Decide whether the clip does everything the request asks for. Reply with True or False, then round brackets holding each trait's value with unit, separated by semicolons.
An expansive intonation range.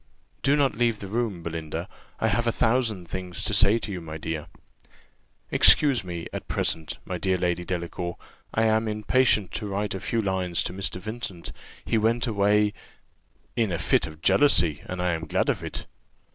False (4.3 semitones)